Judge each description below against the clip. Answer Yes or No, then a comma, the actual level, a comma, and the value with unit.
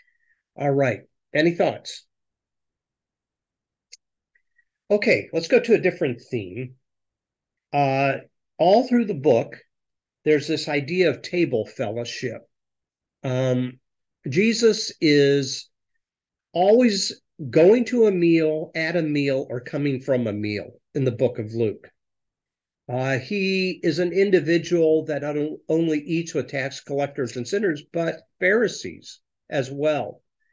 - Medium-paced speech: No, slow, 120 wpm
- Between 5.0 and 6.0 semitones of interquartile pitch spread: Yes, average, 5.3 semitones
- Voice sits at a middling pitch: Yes, medium, 155 Hz